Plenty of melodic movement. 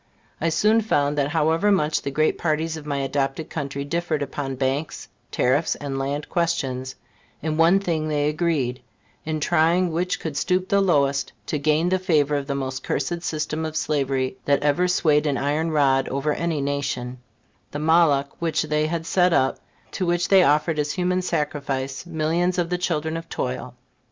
No: average, 3.2 semitones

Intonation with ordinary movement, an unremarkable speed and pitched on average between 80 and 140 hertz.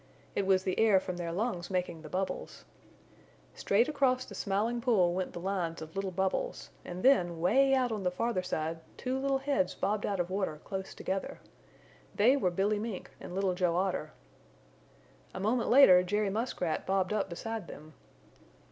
No: average, 4.0 semitones; average, 175 wpm; high, 195 Hz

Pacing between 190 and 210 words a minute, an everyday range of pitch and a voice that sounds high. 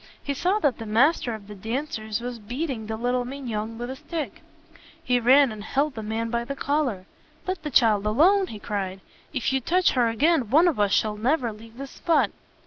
Yes: fast, 205 wpm; average, 4.7 semitones; high, 245 Hz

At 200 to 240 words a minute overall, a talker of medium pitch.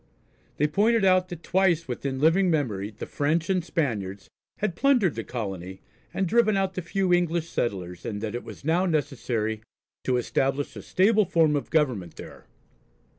No: average, 170 wpm; medium, 155 Hz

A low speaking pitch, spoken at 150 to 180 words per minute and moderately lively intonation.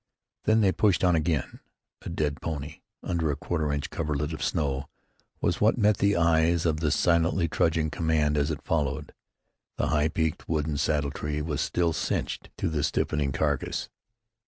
No: very low, 80 Hz; average, 170 wpm; narrow, 2.2 semitones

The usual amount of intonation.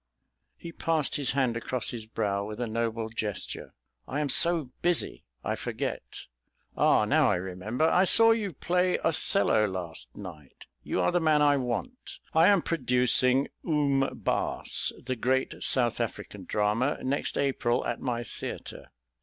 No: wide, 5.9 semitones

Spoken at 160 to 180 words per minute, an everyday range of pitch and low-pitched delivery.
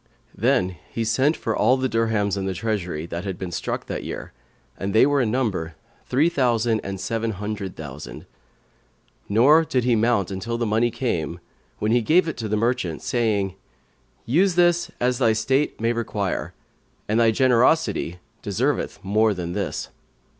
Yes: average, 170 wpm; average, 4.2 semitones; low, 115 Hz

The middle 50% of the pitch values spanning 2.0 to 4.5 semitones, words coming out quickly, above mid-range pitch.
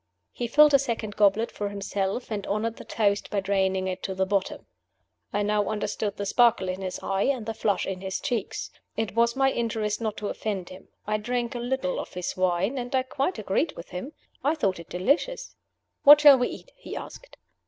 Yes: average, 4.2 semitones; fast, 210 wpm; high, 210 Hz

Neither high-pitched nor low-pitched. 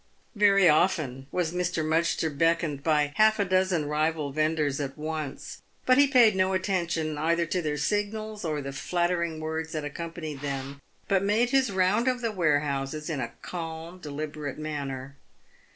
Yes: medium, 160 Hz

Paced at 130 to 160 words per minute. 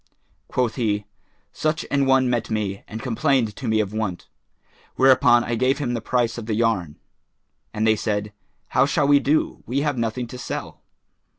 No: average, 180 wpm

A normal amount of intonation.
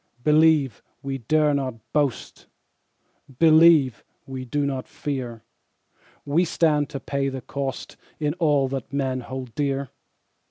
No: narrow, 2.2 semitones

